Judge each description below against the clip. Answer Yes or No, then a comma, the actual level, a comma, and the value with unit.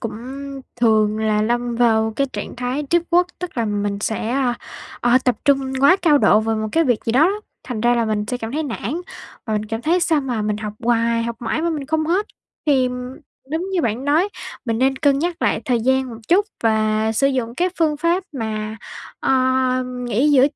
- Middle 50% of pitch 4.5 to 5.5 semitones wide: Yes, average, 4.9 semitones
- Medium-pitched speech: No, high, 245 Hz